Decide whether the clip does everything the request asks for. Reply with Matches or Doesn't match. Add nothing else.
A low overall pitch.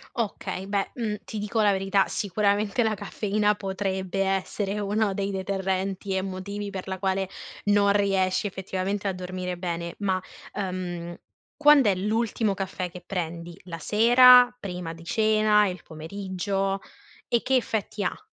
Doesn't match